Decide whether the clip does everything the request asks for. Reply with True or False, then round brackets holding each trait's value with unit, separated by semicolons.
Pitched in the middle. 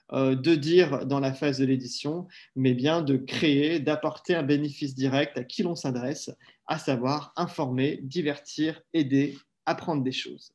True (145 Hz)